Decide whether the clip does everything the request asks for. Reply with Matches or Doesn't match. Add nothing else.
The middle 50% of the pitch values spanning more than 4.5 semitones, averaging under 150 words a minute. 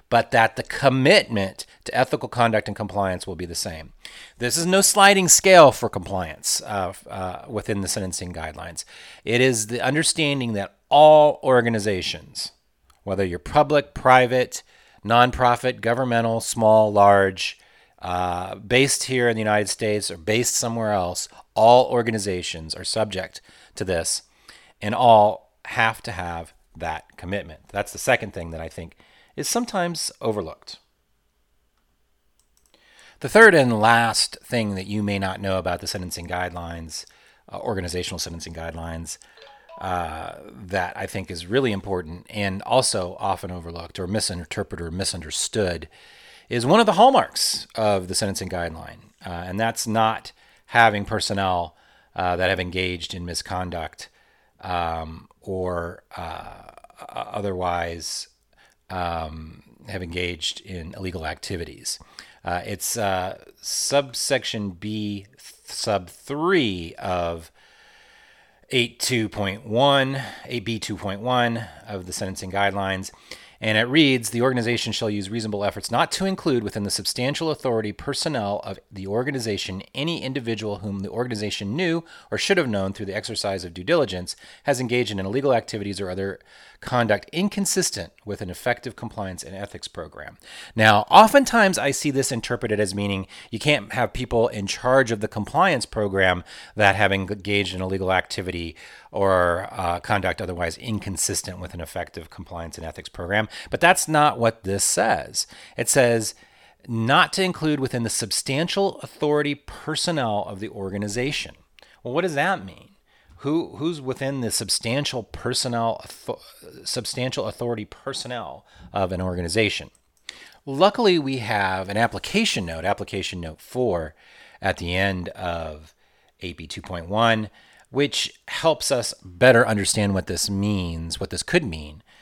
Matches